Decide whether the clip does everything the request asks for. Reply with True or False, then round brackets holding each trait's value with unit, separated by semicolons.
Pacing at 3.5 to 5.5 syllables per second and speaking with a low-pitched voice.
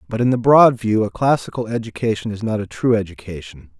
False (5.9 syllables/s; 110 Hz)